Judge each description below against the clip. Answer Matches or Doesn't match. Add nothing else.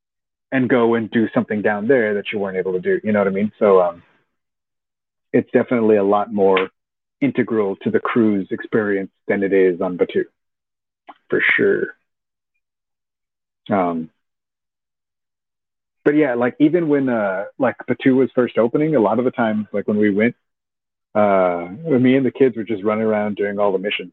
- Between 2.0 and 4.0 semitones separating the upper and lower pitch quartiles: Doesn't match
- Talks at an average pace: Matches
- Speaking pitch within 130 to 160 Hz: Doesn't match